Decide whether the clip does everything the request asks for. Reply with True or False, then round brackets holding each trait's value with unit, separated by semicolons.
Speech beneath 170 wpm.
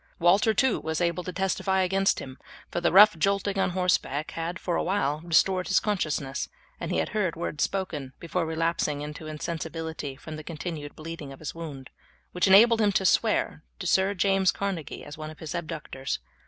False (190 wpm)